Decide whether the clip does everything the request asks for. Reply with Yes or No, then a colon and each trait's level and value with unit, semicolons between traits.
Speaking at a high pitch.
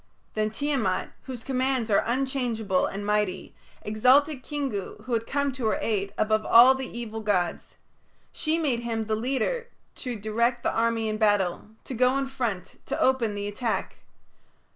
Yes: high, 230 Hz